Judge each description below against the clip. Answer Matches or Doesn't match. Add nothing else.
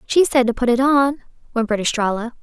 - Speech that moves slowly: Doesn't match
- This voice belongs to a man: Doesn't match